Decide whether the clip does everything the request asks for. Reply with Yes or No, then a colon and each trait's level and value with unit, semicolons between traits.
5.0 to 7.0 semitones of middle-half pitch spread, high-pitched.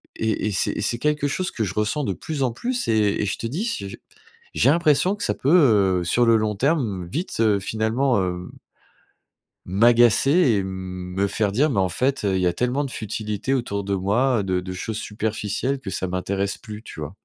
No: wide, 5.4 semitones; low, 110 Hz